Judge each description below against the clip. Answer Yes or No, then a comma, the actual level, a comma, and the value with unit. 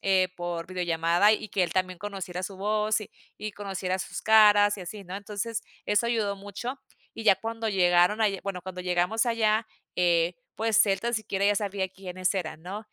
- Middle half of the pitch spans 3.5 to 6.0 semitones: No, average, 2.8 semitones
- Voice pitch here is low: No, high, 195 Hz